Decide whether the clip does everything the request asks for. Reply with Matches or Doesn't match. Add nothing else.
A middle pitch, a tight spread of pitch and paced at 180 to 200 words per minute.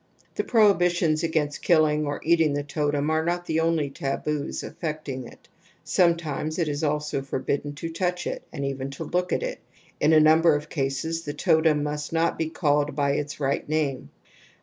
Matches